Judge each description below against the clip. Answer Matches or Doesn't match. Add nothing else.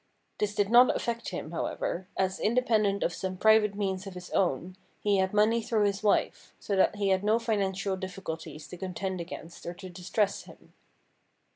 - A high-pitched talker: Matches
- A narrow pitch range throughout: Matches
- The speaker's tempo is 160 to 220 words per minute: Matches